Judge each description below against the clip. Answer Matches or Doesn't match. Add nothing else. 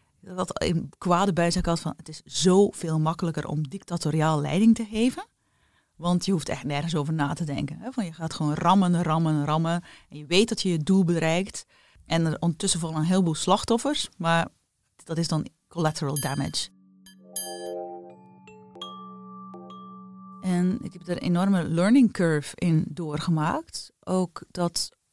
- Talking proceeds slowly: Doesn't match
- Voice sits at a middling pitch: Matches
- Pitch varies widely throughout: Doesn't match